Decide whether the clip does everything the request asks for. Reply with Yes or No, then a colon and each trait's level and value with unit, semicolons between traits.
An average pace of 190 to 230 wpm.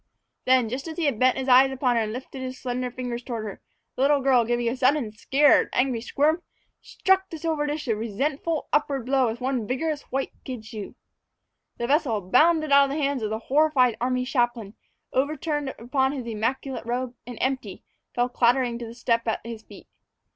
Yes: average, 195 wpm